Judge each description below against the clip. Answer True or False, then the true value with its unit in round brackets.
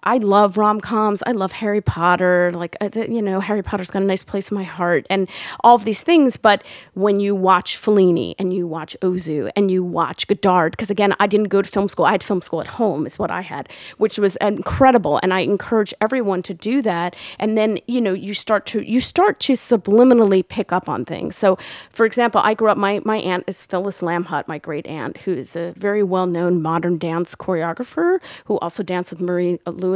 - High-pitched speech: True (195 Hz)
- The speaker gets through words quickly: True (220 wpm)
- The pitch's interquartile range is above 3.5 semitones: False (3.1 semitones)